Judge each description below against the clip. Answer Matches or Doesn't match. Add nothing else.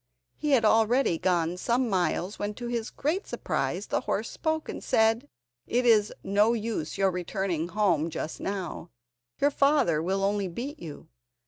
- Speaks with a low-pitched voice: Doesn't match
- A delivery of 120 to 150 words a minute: Doesn't match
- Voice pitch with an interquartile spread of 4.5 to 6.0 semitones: Matches